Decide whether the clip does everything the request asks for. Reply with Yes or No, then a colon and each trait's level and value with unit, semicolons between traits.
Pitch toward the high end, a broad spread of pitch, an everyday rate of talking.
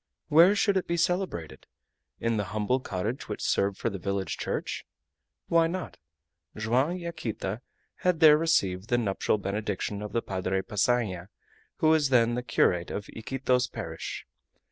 No: low, 115 Hz; wide, 8.0 semitones; average, 155 wpm